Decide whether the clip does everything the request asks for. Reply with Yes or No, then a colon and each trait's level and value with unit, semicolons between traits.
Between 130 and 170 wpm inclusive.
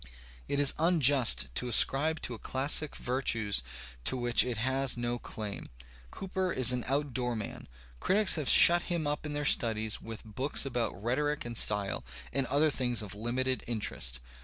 Yes: average, 165 wpm